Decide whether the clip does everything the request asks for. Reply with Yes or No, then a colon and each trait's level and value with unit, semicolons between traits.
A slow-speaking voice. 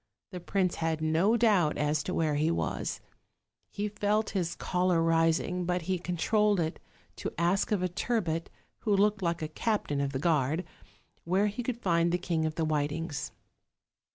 No: average, 175 wpm